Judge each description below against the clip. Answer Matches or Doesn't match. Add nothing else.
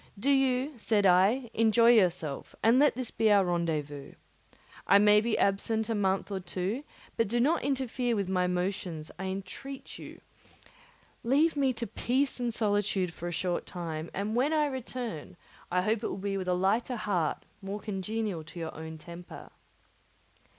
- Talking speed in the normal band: Matches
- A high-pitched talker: Matches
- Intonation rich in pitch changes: Doesn't match